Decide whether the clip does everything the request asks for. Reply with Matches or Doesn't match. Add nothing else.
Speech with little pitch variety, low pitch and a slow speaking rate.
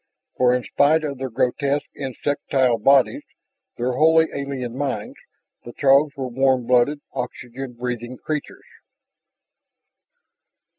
Matches